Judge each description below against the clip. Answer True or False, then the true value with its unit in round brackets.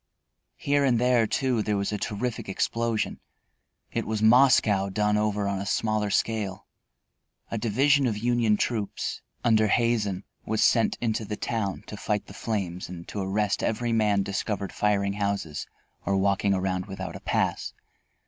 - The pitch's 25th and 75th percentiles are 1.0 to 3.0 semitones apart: True (2.5 semitones)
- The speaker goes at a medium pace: True (160 wpm)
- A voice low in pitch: True (105 Hz)